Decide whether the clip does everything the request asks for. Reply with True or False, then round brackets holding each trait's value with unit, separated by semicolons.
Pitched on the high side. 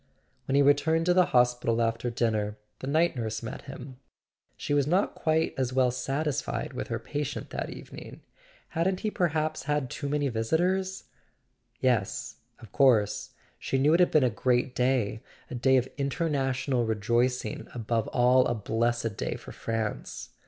False (130 Hz)